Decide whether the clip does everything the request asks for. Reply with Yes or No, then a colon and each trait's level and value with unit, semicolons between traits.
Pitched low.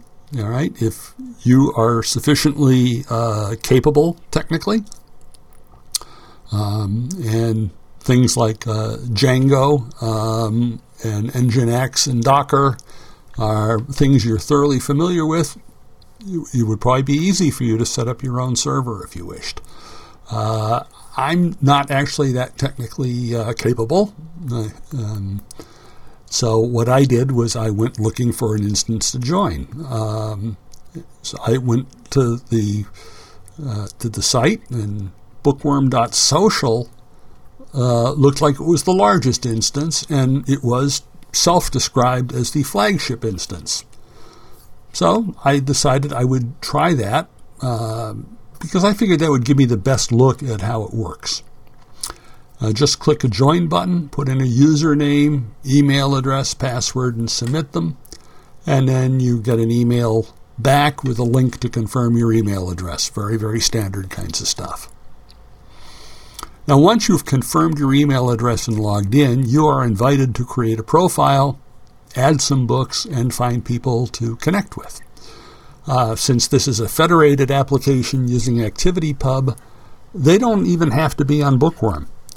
Yes: low, 125 Hz